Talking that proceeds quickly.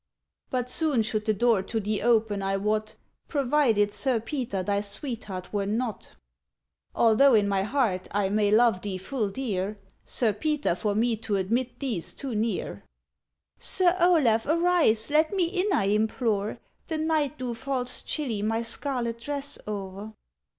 No: average, 155 wpm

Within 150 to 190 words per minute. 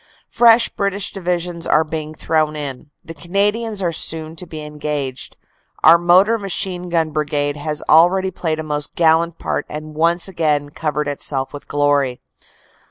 Yes: average, 155 wpm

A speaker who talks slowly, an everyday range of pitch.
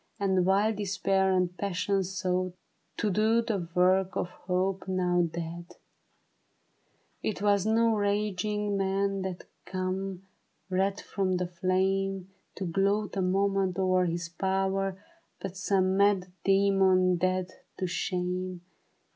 No: slow, 120 wpm; narrow, 1.3 semitones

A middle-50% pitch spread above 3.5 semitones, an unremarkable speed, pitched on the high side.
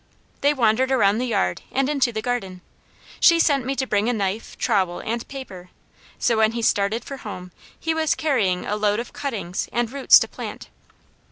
Yes: average, 4.7 semitones; average, 190 wpm; high, 230 Hz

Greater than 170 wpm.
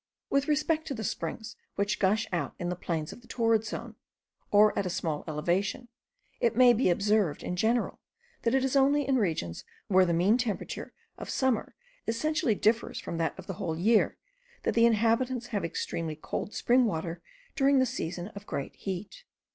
Yes: average, 185 wpm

